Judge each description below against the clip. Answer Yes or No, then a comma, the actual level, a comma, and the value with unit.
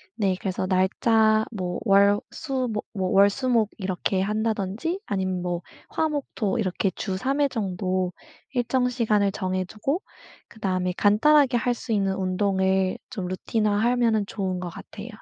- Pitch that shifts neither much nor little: Yes, average, 3.7 semitones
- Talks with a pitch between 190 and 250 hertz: Yes, high, 205 Hz